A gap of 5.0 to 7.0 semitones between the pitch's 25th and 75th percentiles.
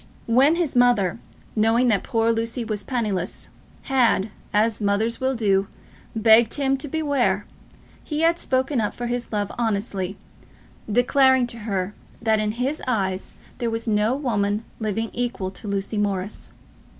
No: average, 3.3 semitones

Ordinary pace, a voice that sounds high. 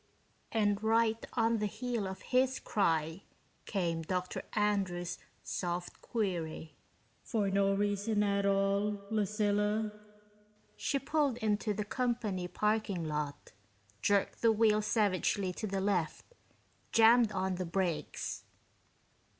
No: slow, 115 wpm; high, 205 Hz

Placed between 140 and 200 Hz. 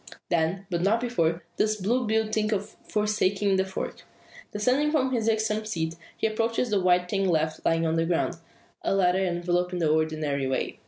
Yes: high, 190 Hz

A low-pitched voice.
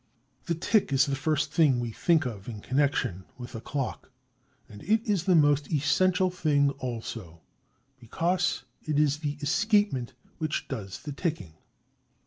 No: medium, 145 Hz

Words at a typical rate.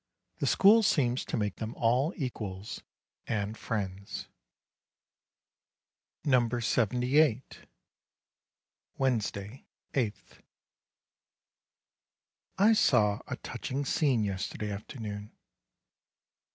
No: slow, 75 wpm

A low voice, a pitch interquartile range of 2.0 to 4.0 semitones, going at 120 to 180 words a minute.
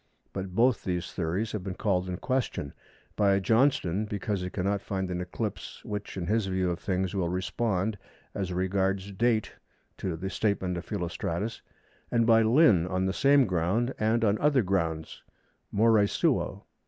Yes: very low, 95 Hz; average, 3.4 semitones; average, 165 wpm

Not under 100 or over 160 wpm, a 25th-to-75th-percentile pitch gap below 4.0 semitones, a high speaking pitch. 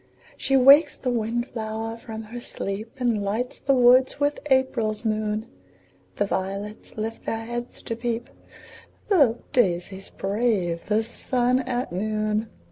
Yes: slow, 135 wpm; narrow, 2.6 semitones; high, 225 Hz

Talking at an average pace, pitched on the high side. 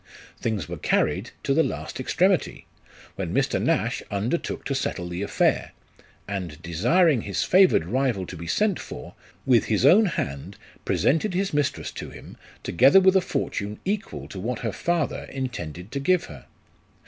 No: average, 160 wpm; low, 125 Hz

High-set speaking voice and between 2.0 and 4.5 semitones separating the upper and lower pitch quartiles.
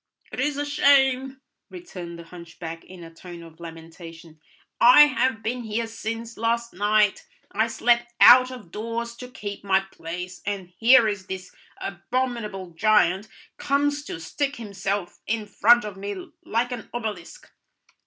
No: high, 215 Hz; average, 5.0 semitones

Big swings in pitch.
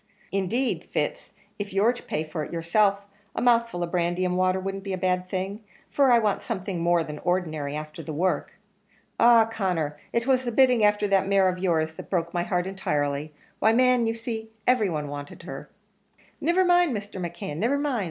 No: average, 4.8 semitones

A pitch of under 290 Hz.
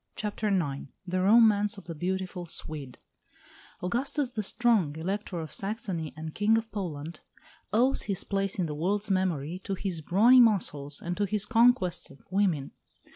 Yes: high, 190 Hz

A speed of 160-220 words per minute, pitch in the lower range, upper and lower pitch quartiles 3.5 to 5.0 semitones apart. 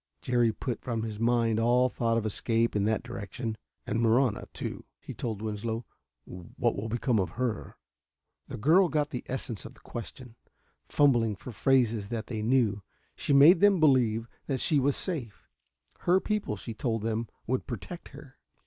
No: average, 170 wpm; low, 115 Hz; average, 3.1 semitones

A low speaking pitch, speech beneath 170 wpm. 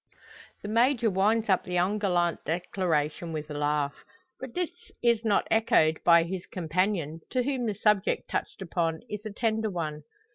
No: high, 190 Hz; average, 160 wpm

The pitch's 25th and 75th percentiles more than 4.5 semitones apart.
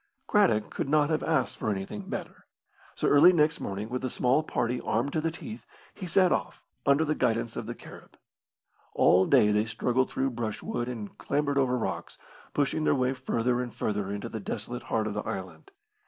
Yes: average, 5.1 semitones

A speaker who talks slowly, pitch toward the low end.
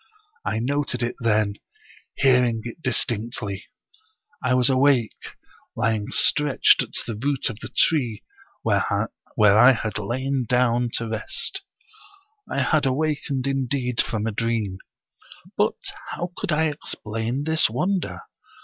Yes: slow, 125 wpm; low, 125 Hz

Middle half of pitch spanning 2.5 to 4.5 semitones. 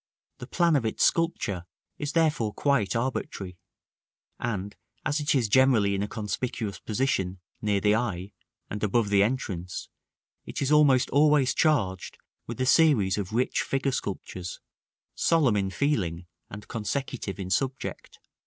No: wide, 5.6 semitones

